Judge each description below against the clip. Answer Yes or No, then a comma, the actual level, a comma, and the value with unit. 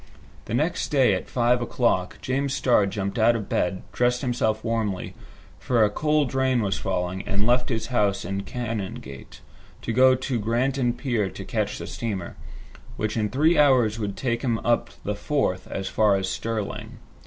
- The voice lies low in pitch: Yes, low, 115 Hz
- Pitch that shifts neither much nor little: Yes, average, 4.0 semitones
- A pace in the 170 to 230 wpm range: Yes, average, 175 wpm